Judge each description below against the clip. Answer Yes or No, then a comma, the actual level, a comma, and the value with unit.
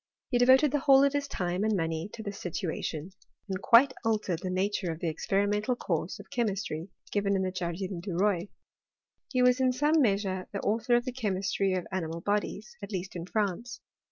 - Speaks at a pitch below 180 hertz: No, high, 200 Hz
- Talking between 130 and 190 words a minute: No, average, 200 wpm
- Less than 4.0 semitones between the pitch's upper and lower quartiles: No, average, 4.6 semitones